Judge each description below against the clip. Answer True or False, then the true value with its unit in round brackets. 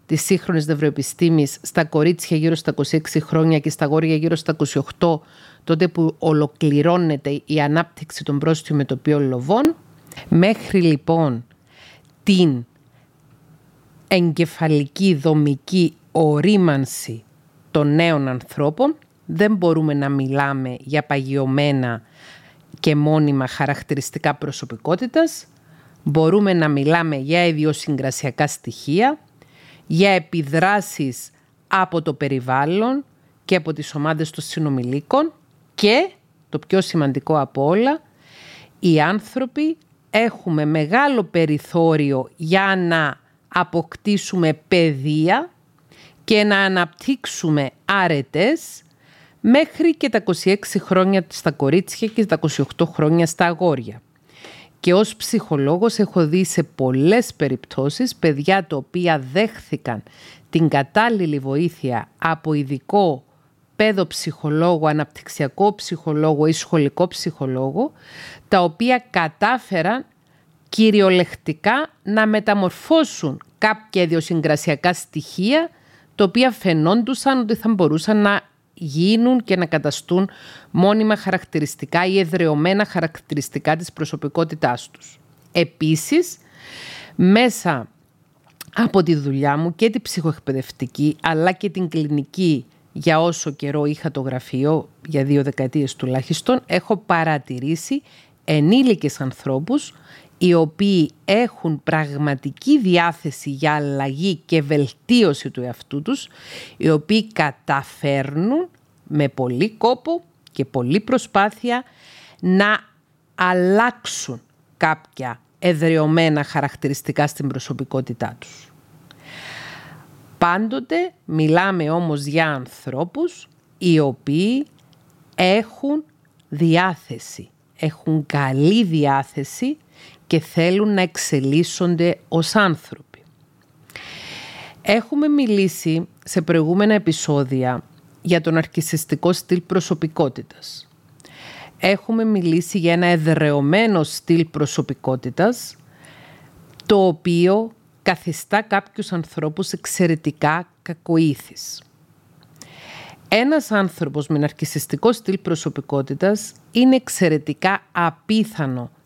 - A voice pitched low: False (160 Hz)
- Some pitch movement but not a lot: True (4.2 semitones)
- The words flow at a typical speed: False (95 wpm)